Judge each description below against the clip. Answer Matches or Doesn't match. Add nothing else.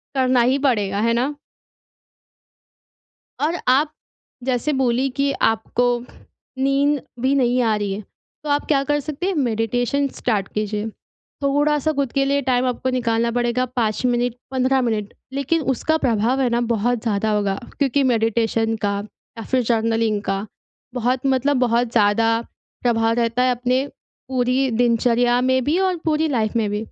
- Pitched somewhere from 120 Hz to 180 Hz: Doesn't match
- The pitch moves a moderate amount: Matches